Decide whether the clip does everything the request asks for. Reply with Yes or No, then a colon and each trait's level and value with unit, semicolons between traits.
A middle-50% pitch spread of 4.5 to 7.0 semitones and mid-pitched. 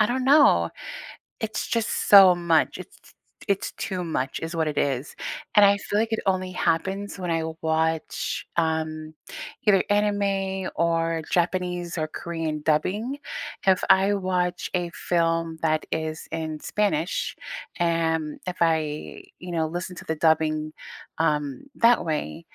No: average, 3.3 semitones; medium, 170 Hz